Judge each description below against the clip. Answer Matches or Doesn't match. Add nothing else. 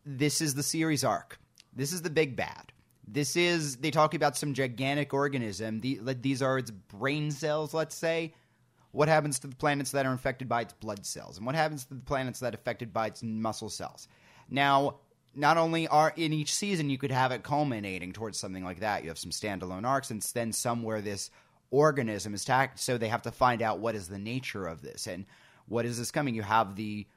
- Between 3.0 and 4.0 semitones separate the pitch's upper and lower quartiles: Doesn't match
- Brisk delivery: Matches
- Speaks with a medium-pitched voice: Doesn't match